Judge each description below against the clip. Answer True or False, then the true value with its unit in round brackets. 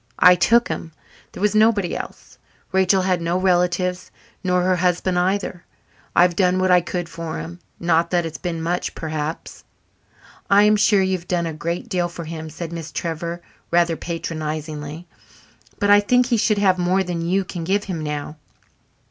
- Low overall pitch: False (175 Hz)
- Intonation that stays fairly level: True (2.1 semitones)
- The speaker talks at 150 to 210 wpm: True (180 wpm)